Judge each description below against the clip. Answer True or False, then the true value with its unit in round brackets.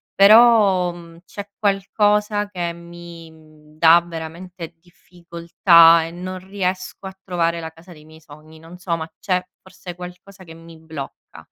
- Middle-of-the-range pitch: True (175 Hz)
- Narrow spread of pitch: True (2.3 semitones)